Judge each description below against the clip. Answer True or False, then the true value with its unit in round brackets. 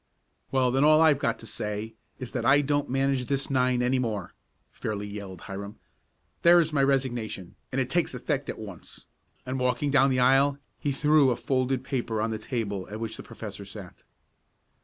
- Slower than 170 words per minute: False (185 wpm)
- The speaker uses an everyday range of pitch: True (3.9 semitones)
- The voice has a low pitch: True (125 Hz)